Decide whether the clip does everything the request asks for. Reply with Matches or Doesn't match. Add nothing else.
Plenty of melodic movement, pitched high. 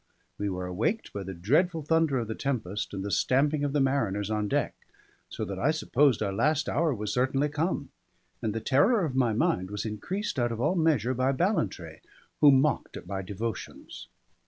Doesn't match